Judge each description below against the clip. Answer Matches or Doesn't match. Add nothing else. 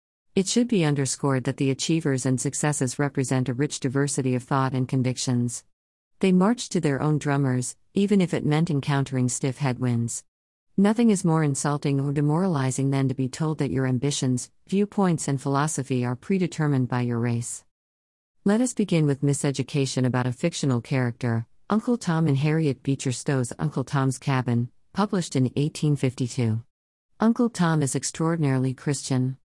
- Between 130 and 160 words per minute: Matches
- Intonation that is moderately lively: Matches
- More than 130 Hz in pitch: Matches